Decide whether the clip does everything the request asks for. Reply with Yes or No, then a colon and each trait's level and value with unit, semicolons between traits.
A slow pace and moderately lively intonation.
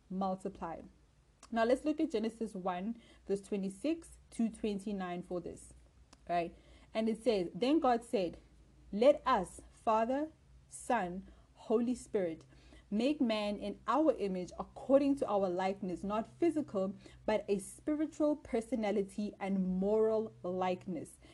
Yes: slow, 125 wpm; average, 4.5 semitones